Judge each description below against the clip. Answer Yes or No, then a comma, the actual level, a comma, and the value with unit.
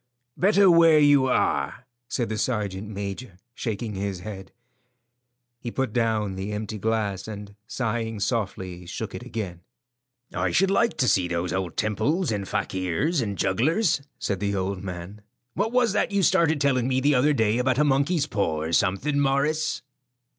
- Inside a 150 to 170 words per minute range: Yes, average, 165 wpm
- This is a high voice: No, low, 110 Hz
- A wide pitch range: Yes, wide, 6.5 semitones